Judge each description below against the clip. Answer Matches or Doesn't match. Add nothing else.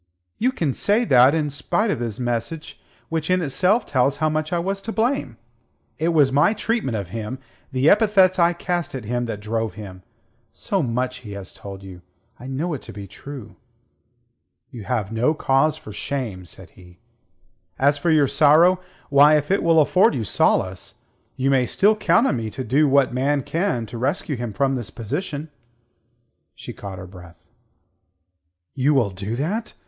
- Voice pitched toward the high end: Doesn't match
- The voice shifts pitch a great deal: Matches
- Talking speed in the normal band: Matches